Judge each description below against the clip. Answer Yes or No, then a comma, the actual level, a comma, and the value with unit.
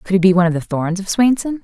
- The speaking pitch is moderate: No, high, 195 Hz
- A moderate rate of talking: No, fast, 330 wpm